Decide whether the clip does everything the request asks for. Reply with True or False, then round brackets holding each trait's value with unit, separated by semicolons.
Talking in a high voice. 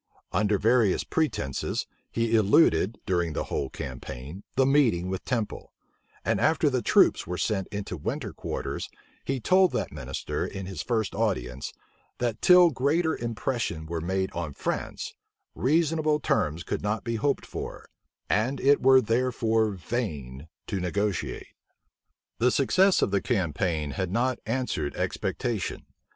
False (110 Hz)